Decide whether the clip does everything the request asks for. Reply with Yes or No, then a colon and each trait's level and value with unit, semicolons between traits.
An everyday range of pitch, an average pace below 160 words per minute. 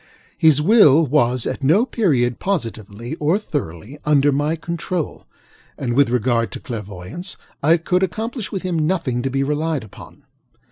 No: wide, 5.7 semitones; average, 150 wpm